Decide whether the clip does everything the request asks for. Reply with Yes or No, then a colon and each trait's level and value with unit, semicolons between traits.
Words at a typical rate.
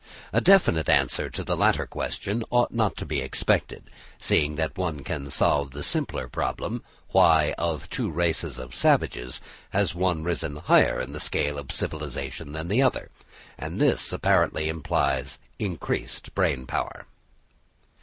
Yes: average, 155 wpm